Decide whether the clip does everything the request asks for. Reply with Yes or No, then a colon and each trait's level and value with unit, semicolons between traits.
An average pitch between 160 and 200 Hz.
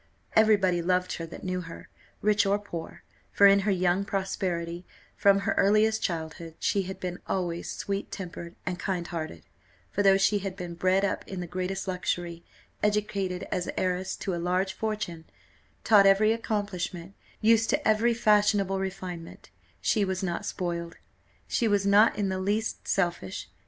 Yes: high, 190 Hz